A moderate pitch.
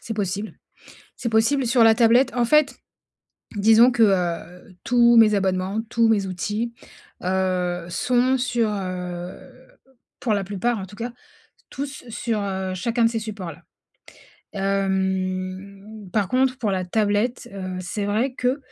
No: high, 210 Hz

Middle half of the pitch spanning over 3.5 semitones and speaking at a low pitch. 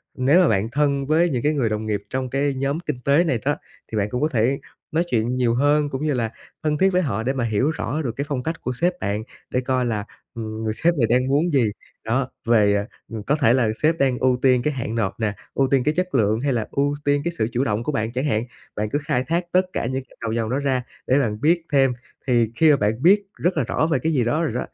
Yes: average, 4.5 semitones; low, 130 Hz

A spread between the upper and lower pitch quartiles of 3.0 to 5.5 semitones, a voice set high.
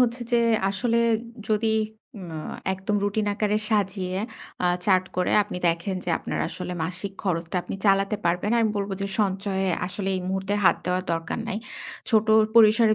No: narrow, 2.5 semitones; high, 195 Hz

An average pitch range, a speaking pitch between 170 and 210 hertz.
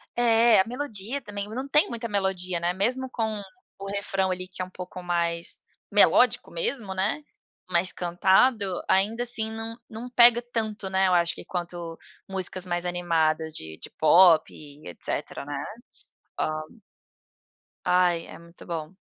Yes: average, 4.4 semitones; high, 190 Hz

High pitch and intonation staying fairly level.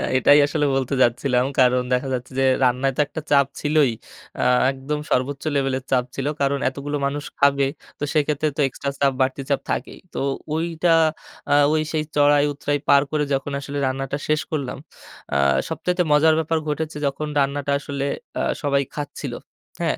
No: medium, 140 Hz; narrow, 1.7 semitones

